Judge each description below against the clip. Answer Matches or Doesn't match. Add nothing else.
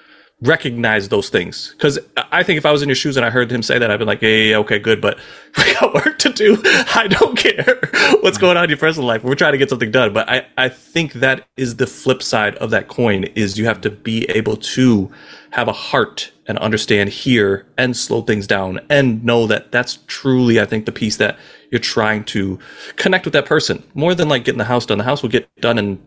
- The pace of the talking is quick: Matches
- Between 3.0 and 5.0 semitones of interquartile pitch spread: Matches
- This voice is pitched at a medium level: Doesn't match